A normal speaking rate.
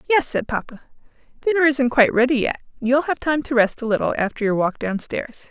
No: fast, 220 wpm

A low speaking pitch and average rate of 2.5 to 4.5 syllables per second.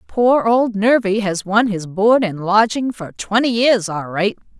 No: high, 210 Hz; 4.0 syllables/s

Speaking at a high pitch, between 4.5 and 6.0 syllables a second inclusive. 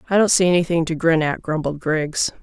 No: medium, 165 Hz; 5.6 syllables/s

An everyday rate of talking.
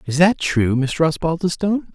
Yes: average, 155 wpm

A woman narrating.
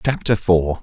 No: male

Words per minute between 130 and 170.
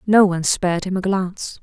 No: fast, 220 wpm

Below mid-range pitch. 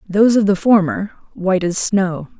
No: high, 195 Hz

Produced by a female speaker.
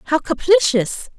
Yes: female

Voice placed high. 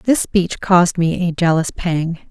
No: medium, 175 Hz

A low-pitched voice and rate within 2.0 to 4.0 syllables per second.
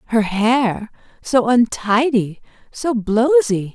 No: high, 230 Hz; 3.1 syllables/s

